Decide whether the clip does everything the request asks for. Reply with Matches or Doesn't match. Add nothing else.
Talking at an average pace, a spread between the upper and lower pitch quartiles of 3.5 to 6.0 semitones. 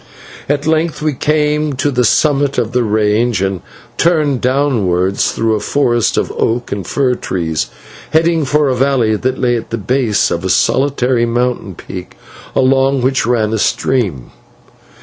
Matches